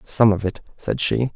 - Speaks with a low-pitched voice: Yes, low, 110 Hz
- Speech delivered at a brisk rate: Yes, fast, 220 wpm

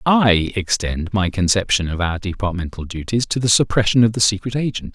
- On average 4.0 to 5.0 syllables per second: No, 5.4 syllables/s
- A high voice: No, low, 100 Hz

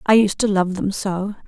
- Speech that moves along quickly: Yes, fast, 245 wpm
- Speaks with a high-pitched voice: Yes, high, 195 Hz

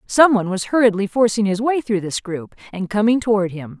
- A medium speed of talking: No, fast, 220 wpm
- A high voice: Yes, high, 210 Hz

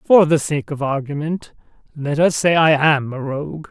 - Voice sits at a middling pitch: Yes, medium, 150 Hz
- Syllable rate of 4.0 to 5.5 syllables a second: Yes, 4.7 syllables/s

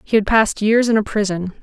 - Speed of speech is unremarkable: No, fast, 260 wpm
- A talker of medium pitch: No, high, 210 Hz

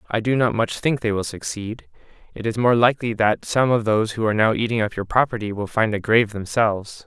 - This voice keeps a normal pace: No, fast, 240 wpm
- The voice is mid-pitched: No, low, 110 Hz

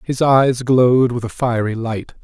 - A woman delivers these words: No, male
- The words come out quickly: No, average, 190 wpm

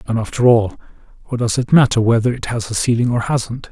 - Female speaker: No, male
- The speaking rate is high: Yes, fast, 225 wpm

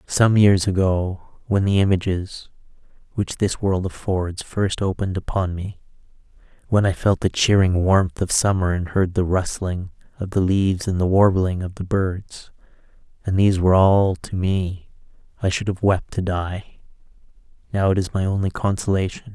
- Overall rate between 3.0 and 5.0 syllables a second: Yes, 4.7 syllables/s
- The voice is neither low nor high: No, very low, 95 Hz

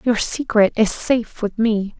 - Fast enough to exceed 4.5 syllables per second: No, 4.3 syllables/s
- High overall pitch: Yes, high, 225 Hz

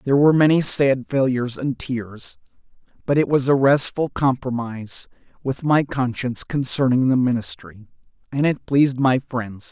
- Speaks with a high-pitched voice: No, low, 130 Hz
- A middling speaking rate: Yes, average, 150 wpm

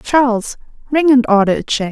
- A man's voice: No, female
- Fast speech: No, average, 190 wpm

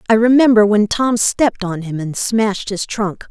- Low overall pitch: No, high, 215 Hz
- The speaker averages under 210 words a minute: Yes, average, 200 wpm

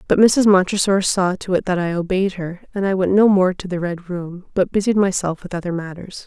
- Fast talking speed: Yes, fast, 240 wpm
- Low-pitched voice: No, medium, 185 Hz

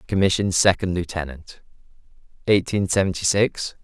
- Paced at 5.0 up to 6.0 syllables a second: Yes, 5.4 syllables/s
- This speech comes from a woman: No, male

